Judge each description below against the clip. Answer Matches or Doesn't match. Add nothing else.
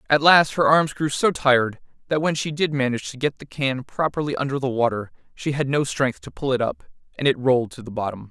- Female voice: Doesn't match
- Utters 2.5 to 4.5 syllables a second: Doesn't match